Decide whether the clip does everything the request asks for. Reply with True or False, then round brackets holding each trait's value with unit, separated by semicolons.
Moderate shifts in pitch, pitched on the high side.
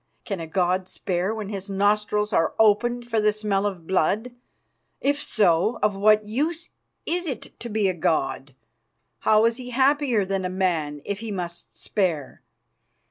True (3.5 semitones; 205 Hz)